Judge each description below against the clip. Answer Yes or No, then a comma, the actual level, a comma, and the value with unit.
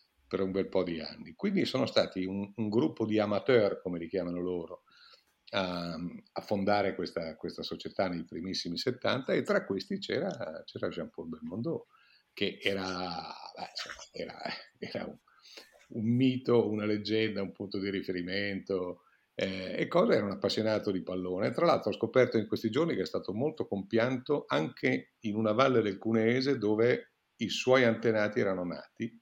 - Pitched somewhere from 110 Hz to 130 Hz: No, low, 100 Hz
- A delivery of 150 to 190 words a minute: Yes, average, 160 wpm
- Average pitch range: Yes, average, 3.2 semitones